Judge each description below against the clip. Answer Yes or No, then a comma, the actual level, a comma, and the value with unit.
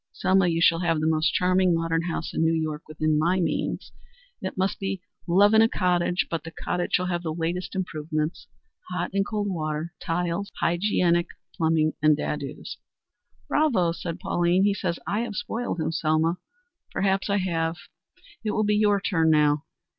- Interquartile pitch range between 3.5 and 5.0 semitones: No, average, 2.8 semitones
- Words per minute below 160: No, average, 175 wpm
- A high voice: No, medium, 175 Hz